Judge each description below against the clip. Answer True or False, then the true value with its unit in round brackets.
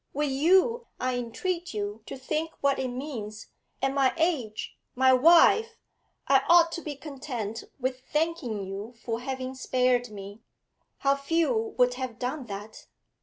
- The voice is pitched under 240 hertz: False (260 Hz)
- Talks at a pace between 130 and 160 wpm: True (150 wpm)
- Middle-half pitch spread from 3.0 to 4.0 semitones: False (4.8 semitones)